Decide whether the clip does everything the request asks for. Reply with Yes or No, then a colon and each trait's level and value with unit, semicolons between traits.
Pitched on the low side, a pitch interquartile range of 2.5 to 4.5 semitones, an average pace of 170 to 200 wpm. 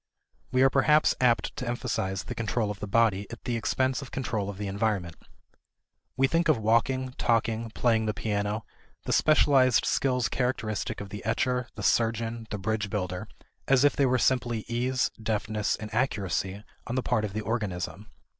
Yes: low, 115 Hz; average, 3.4 semitones; average, 175 wpm